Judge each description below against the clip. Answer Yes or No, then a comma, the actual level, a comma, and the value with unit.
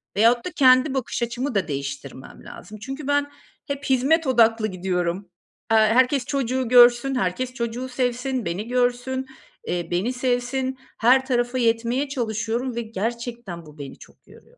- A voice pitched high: Yes, high, 245 Hz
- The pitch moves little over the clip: No, average, 3.1 semitones